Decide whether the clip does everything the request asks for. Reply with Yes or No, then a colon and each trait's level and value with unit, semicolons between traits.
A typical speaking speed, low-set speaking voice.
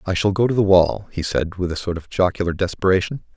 No: fast, 250 wpm; very low, 95 Hz